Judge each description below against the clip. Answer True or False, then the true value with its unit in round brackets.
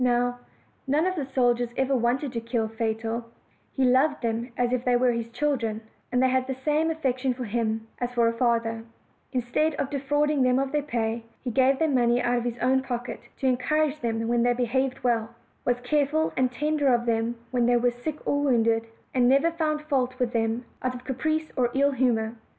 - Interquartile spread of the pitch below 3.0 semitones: True (2.5 semitones)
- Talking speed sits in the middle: False (210 wpm)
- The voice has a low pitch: False (250 Hz)